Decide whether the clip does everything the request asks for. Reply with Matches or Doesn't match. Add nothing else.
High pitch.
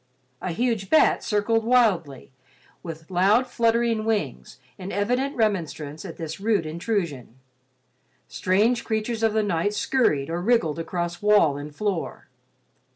Matches